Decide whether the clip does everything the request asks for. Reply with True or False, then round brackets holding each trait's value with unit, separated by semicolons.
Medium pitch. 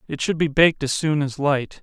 True (145 Hz)